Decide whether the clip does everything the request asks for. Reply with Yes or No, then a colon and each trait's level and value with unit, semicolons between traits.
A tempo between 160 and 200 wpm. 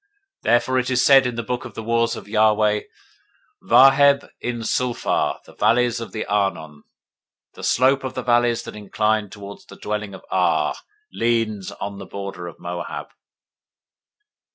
Yes: average, 165 wpm